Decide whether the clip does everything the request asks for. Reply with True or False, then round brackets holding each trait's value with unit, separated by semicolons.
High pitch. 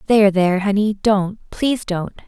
True (200 Hz)